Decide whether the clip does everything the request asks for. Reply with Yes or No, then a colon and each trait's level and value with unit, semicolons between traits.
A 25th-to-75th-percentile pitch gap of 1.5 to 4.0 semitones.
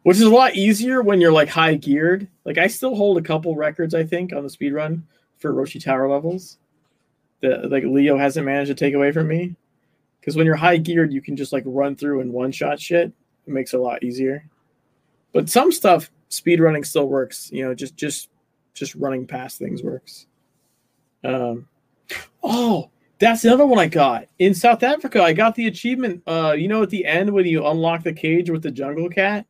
No: average, 4.5 semitones